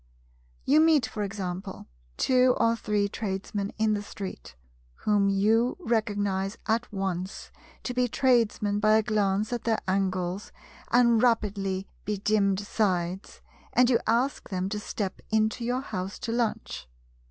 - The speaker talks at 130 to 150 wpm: Yes, average, 140 wpm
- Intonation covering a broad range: No, average, 3.0 semitones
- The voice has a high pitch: Yes, high, 210 Hz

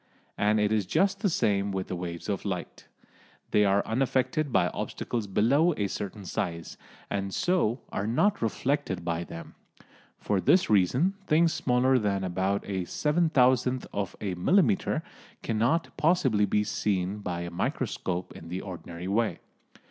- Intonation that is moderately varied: No, wide, 6.1 semitones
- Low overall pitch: Yes, low, 105 Hz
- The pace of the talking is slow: No, average, 155 wpm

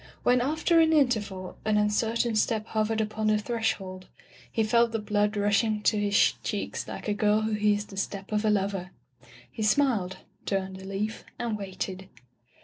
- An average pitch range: No, narrow, 1.8 semitones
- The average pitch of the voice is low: No, high, 210 Hz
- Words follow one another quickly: No, average, 175 wpm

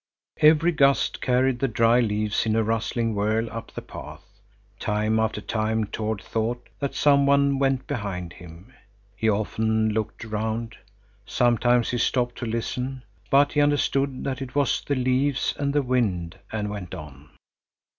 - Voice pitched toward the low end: Yes, low, 115 Hz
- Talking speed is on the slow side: No, average, 155 wpm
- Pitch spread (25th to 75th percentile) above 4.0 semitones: No, average, 3.7 semitones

